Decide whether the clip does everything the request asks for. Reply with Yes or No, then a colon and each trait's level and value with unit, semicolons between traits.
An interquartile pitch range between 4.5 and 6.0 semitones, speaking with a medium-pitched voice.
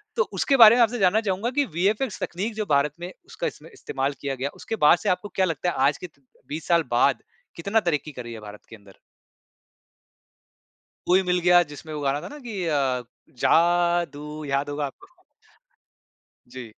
Yes: wide, 5.6 semitones; medium, 170 Hz